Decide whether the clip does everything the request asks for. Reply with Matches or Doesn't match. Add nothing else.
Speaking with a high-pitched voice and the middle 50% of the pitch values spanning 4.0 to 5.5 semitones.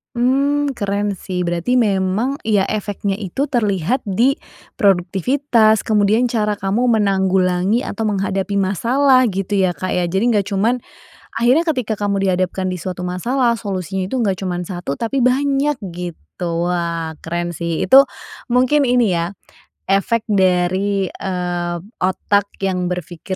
Matches